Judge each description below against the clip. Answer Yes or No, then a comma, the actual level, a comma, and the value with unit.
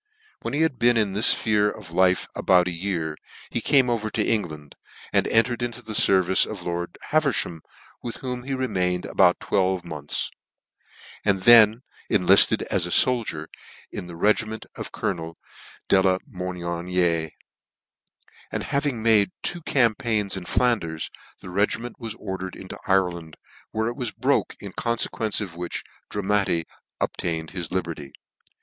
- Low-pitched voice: Yes, very low, 95 Hz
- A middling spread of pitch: Yes, average, 4.6 semitones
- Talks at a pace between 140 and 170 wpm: Yes, average, 155 wpm